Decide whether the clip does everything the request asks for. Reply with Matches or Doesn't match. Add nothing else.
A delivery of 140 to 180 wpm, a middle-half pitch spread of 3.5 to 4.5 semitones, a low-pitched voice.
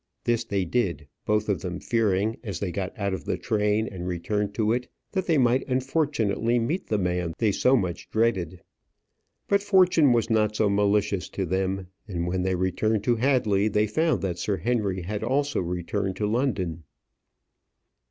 Matches